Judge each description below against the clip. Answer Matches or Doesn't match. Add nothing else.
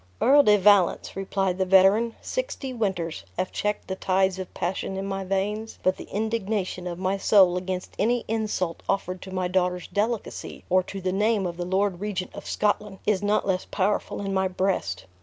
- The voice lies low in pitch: Doesn't match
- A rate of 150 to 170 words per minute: Doesn't match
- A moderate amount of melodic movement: Doesn't match